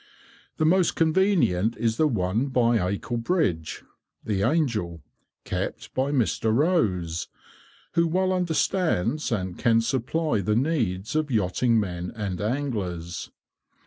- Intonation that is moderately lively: No, wide, 8.7 semitones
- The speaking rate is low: Yes, slow, 120 wpm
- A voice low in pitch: Yes, low, 115 Hz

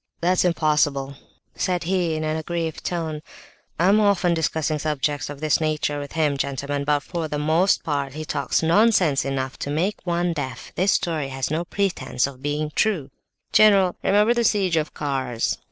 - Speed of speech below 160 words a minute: No, average, 175 wpm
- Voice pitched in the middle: Yes, medium, 155 Hz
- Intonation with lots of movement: No, average, 3.7 semitones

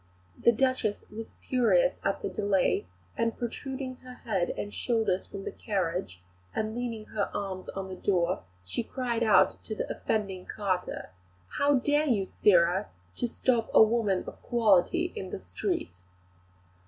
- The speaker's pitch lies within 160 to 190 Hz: No, high, 215 Hz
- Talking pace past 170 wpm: No, average, 155 wpm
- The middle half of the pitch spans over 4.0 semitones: Yes, average, 4.4 semitones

